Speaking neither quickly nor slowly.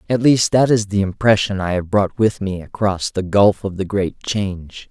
No: fast, 220 wpm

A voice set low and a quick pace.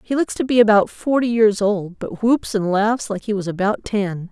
No: high, 210 Hz; fast, 235 wpm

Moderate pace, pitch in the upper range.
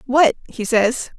Yes: average, 150 wpm; high, 245 Hz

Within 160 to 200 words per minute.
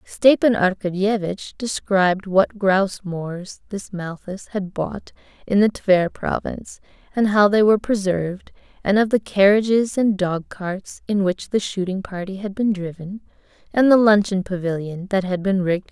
Yes: average, 170 wpm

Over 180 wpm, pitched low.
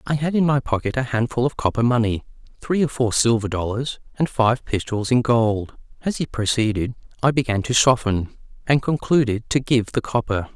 Yes: average, 190 wpm; low, 120 Hz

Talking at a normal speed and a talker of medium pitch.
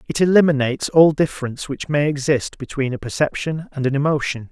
Yes: average, 175 wpm; medium, 145 Hz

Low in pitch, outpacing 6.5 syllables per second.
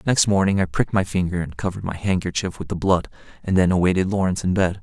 Yes: very low, 95 Hz; 6.9 syllables/s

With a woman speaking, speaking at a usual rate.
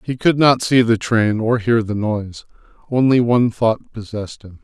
No: male; average, 195 wpm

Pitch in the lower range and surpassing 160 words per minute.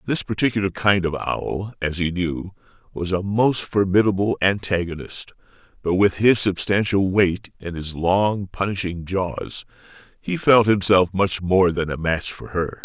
No: very low, 95 Hz; average, 155 wpm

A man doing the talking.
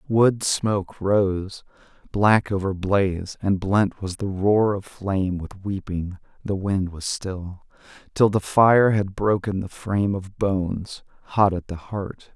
Yes: male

